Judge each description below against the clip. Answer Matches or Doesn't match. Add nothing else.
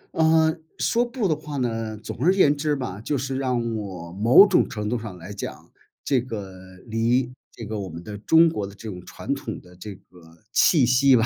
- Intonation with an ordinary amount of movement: Doesn't match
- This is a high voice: Doesn't match